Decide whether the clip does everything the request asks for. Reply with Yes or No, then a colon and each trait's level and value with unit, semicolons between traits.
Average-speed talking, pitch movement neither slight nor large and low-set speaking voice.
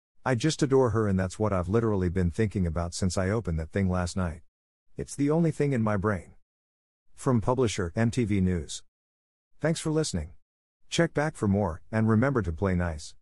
No: average, 190 wpm; wide, 5.7 semitones; low, 100 Hz